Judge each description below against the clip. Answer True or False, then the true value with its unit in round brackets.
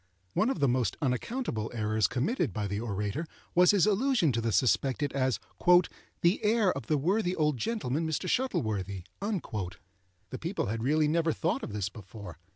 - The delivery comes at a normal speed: True (165 wpm)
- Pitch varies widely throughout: True (8.8 semitones)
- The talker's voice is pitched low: True (130 Hz)